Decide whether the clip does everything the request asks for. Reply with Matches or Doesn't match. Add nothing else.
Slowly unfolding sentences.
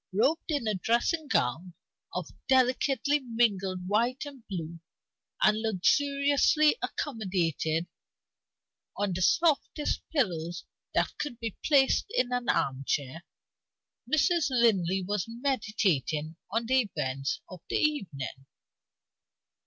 Matches